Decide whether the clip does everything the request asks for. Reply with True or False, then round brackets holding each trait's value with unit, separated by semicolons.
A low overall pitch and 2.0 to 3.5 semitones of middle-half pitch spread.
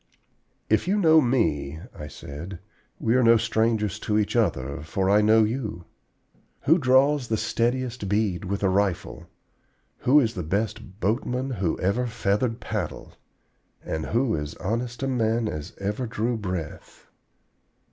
False (110 Hz; 4.1 semitones)